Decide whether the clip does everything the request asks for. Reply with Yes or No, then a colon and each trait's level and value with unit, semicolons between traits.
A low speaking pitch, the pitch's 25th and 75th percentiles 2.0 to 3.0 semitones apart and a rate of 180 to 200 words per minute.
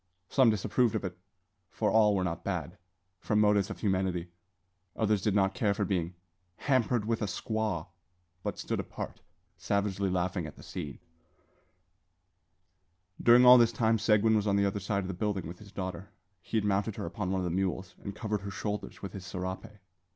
Yes: low, 100 Hz; narrow, 2.6 semitones; average, 190 wpm